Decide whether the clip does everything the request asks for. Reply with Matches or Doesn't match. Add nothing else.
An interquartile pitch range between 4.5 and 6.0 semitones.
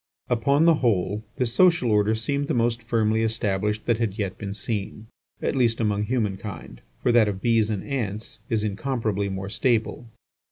Doesn't match